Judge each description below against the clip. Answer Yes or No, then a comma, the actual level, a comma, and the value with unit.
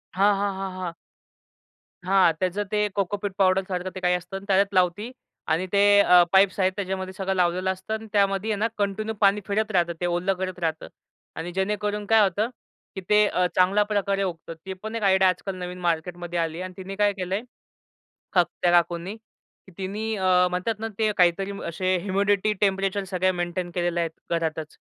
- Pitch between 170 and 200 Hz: Yes, high, 190 Hz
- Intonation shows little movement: Yes, narrow, 2.1 semitones